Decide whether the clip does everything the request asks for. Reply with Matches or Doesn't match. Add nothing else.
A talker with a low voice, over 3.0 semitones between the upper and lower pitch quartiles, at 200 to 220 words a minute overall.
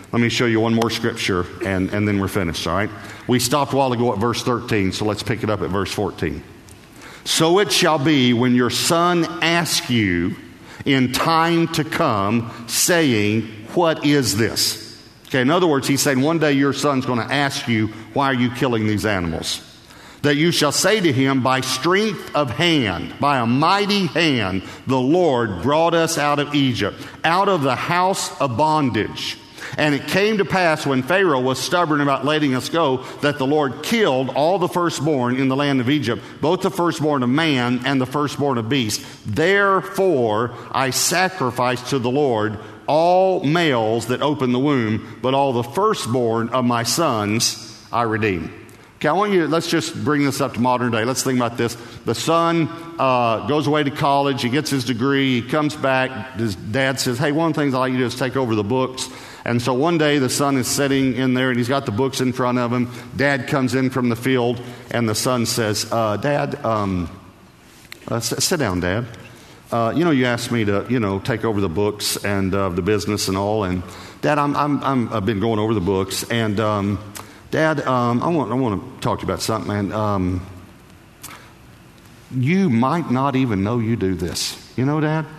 Matches